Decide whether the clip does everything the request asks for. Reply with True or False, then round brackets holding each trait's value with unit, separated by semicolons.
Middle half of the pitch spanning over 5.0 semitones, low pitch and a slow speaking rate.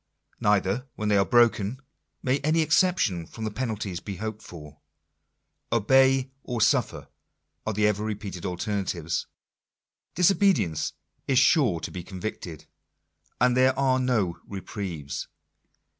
True (5.4 semitones; 105 Hz; 125 wpm)